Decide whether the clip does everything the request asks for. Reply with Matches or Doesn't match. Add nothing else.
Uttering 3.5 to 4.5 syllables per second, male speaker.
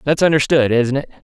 Doesn't match